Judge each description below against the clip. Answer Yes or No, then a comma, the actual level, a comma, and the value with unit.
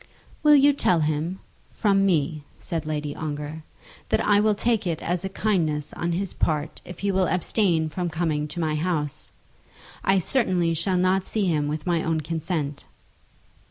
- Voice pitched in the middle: Yes, medium, 170 Hz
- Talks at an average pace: Yes, average, 170 wpm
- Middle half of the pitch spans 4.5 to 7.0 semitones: No, average, 3.8 semitones